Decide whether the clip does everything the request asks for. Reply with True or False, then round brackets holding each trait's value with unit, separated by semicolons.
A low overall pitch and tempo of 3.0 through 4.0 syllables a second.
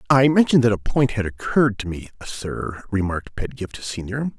False (115 Hz; 5.4 syllables/s)